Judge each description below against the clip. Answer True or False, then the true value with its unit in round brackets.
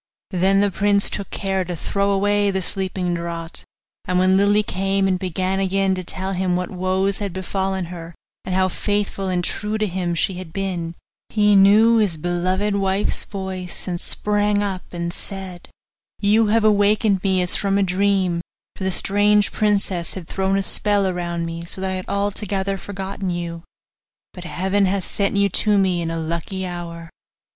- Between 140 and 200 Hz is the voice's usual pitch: True (190 Hz)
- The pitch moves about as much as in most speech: False (1.9 semitones)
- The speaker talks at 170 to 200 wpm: True (180 wpm)